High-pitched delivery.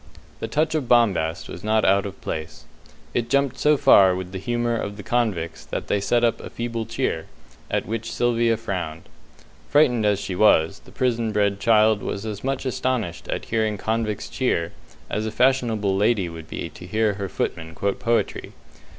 No: low, 110 Hz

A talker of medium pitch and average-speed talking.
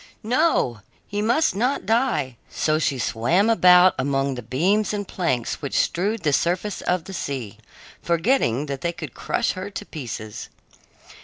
Yes: medium, 170 Hz; average, 155 wpm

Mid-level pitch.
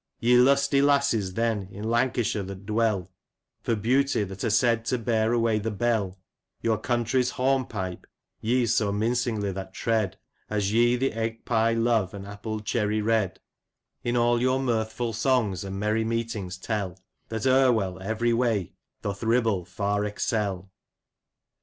No: low, 110 Hz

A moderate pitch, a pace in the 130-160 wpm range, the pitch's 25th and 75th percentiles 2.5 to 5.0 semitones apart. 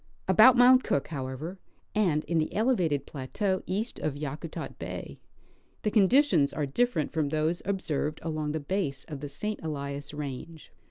No: medium, 160 Hz; average, 155 wpm; wide, 5.6 semitones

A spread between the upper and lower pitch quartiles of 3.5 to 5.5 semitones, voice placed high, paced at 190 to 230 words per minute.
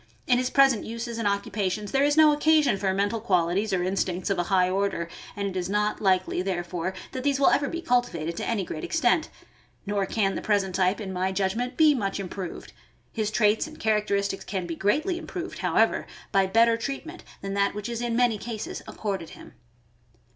Yes: average, 4.2 semitones; high, 205 Hz; average, 195 wpm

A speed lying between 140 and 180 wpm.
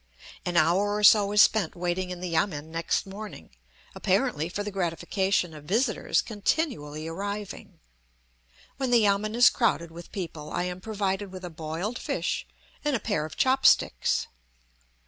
Yes: average, 160 wpm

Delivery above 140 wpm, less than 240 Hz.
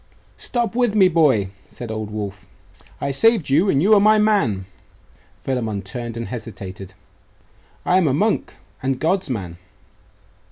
Yes: average, 150 wpm; low, 135 Hz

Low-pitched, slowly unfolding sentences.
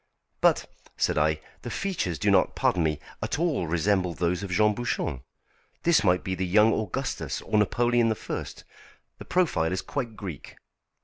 No: low, 100 Hz; average, 165 wpm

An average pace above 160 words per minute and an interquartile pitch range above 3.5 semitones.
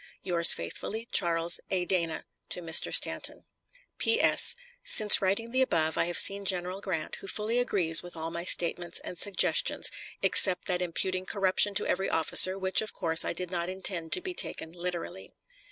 No: average, 170 wpm; average, 2.7 semitones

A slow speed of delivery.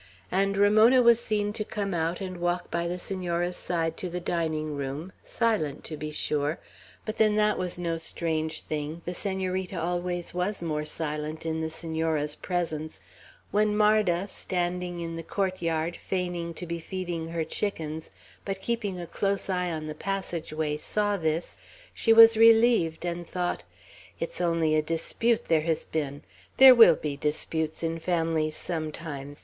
No: average, 165 wpm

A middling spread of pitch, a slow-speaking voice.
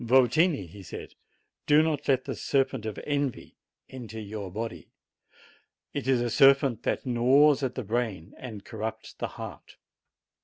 No: average, 3.9 semitones; average, 165 wpm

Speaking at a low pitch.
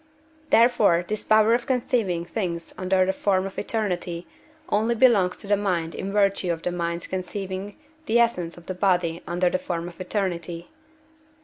No: medium, 185 Hz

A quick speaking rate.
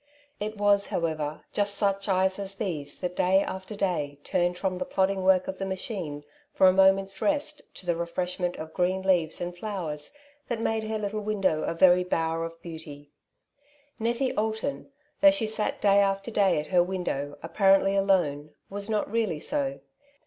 No: average, 175 wpm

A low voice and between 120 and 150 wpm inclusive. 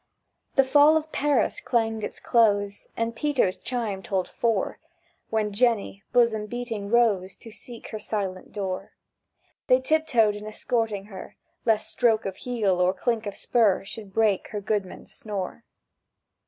No: high, 220 Hz; average, 145 wpm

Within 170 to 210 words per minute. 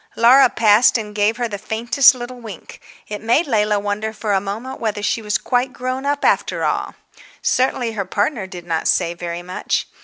Yes: average, 190 wpm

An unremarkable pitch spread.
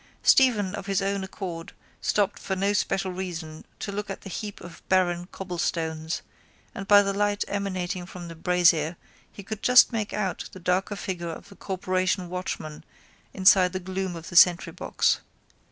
No: narrow, 2.2 semitones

